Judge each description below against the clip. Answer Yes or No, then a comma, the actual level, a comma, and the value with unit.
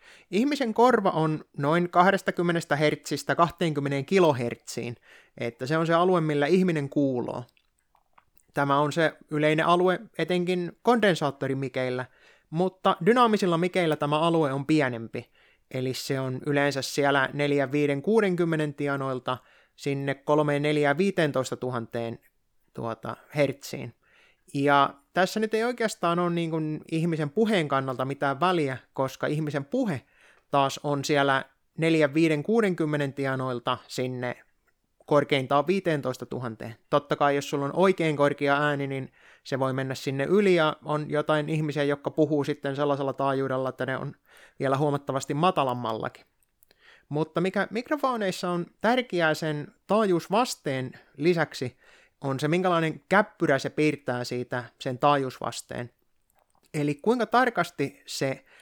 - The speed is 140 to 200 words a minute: No, average, 120 wpm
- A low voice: No, medium, 150 Hz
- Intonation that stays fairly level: No, average, 4.3 semitones